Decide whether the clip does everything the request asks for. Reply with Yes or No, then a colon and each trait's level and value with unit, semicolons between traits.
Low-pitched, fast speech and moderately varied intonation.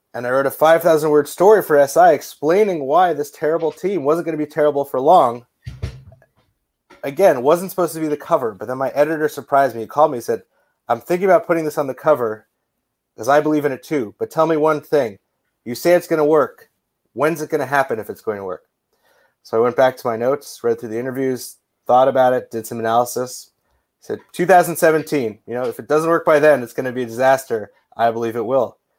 No: medium, 145 Hz; fast, 230 wpm; average, 3.9 semitones